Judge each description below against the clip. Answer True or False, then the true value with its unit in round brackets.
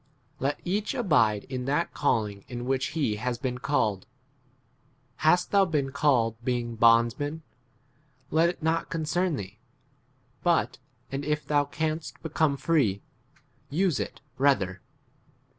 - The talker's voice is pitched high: False (140 Hz)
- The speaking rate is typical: False (130 wpm)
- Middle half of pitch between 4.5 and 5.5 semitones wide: True (5.2 semitones)